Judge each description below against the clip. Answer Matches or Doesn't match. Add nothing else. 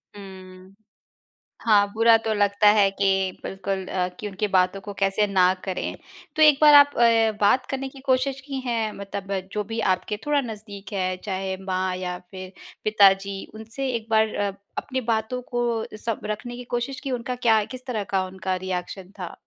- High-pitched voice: Matches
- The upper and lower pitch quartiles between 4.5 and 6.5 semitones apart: Doesn't match